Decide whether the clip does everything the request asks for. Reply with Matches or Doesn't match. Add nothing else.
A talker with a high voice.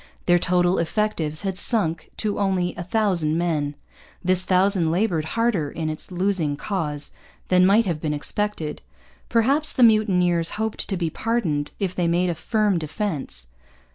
Doesn't match